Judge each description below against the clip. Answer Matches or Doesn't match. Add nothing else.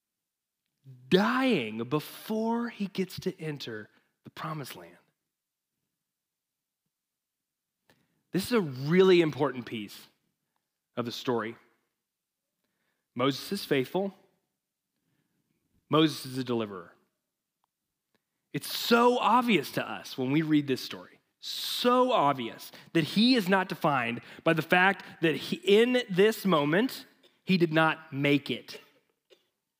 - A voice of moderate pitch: Matches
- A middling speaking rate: Doesn't match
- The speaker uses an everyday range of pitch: Doesn't match